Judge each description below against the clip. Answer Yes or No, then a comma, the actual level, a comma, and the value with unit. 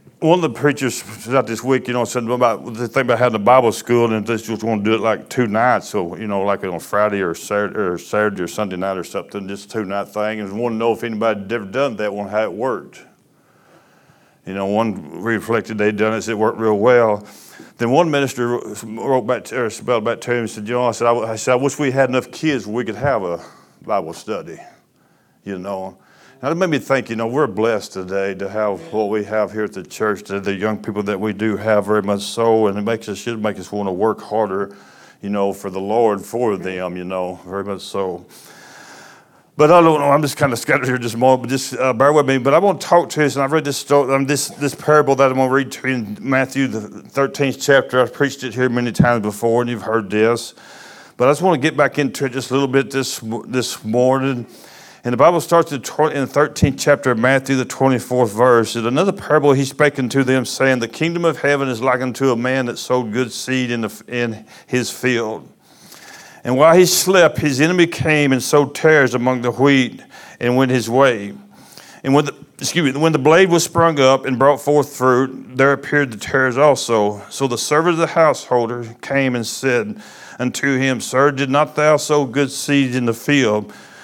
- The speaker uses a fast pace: Yes, fast, 240 wpm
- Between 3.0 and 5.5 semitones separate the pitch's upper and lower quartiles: Yes, average, 4.1 semitones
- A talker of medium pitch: No, low, 125 Hz